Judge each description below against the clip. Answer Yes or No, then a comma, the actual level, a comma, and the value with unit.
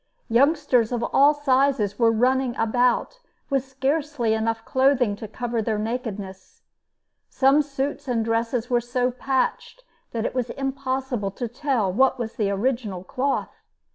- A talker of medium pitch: No, high, 245 Hz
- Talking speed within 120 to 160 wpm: Yes, average, 140 wpm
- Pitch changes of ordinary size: Yes, average, 3.1 semitones